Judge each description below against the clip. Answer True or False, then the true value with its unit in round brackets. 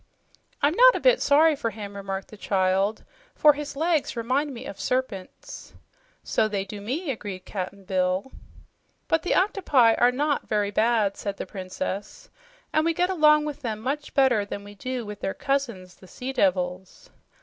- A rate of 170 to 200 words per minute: True (175 wpm)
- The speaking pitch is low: False (230 Hz)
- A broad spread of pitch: True (6.7 semitones)